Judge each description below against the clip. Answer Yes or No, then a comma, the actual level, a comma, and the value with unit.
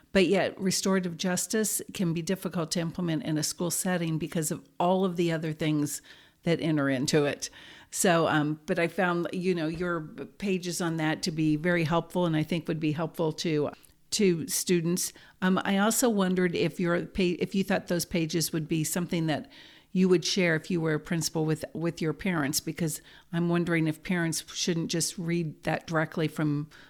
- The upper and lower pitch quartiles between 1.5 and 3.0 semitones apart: Yes, narrow, 2.4 semitones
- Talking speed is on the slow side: No, average, 195 wpm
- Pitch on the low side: No, medium, 170 Hz